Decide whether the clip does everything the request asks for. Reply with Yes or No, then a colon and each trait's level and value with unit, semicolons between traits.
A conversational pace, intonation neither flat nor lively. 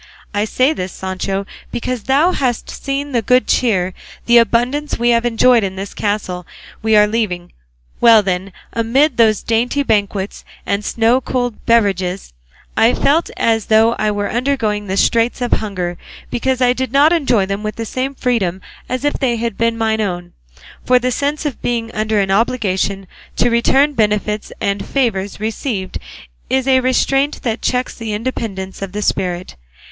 Yes: average, 170 wpm; average, 3.9 semitones